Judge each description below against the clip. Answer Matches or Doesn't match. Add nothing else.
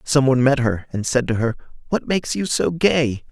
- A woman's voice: Doesn't match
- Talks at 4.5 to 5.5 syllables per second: Matches